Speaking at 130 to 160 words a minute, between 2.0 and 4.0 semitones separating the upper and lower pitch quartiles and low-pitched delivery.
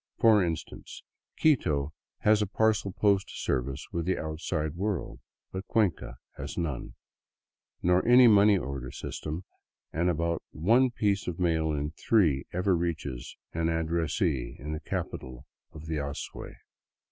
No: slow, 135 wpm; average, 4.6 semitones; very low, 85 Hz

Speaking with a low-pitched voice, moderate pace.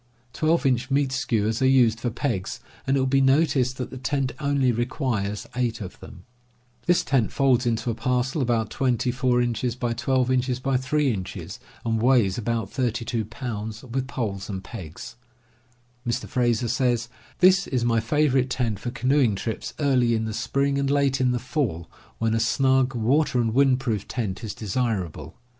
Yes: low, 125 Hz; average, 160 wpm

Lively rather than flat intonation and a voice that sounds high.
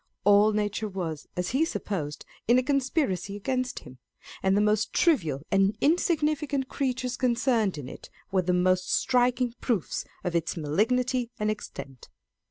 Yes: wide, 5.7 semitones; high, 215 Hz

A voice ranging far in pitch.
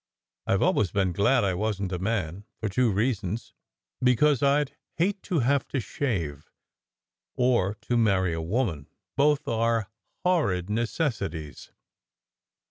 Yes: wide, 5.8 semitones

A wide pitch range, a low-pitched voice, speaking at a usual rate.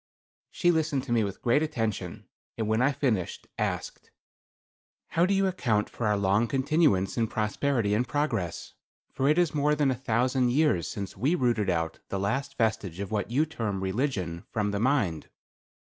Yes: wide, 5.7 semitones; low, 120 Hz; average, 180 wpm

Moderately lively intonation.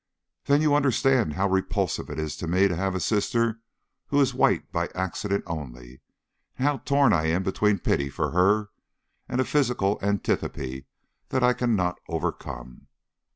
No: wide, 7.1 semitones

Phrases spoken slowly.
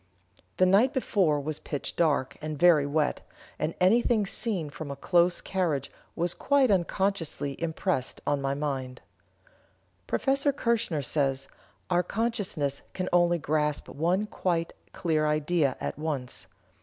Yes: slow, 130 wpm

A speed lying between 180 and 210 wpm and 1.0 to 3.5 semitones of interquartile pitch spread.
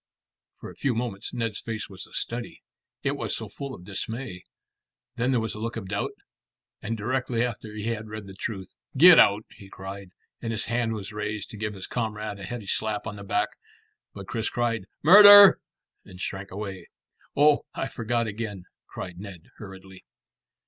Yes: average, 185 wpm; average, 2.9 semitones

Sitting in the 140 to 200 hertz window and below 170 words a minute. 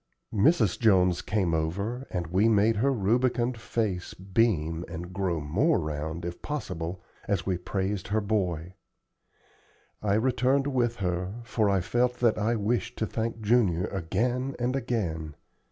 No: low, 105 Hz; average, 150 wpm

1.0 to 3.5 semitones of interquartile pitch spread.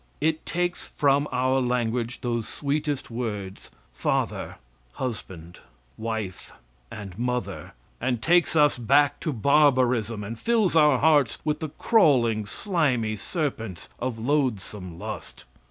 No: average, 5.0 semitones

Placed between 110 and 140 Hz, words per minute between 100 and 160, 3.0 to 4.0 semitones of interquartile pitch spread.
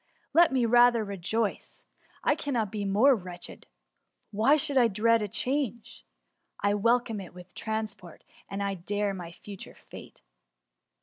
No: high, 215 Hz; slow, 135 wpm; average, 3.5 semitones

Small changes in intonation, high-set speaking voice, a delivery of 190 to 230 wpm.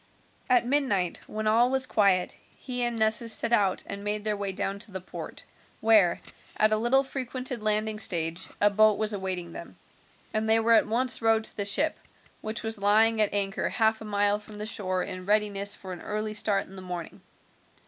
Yes: narrow, 2.1 semitones; high, 215 Hz; average, 200 wpm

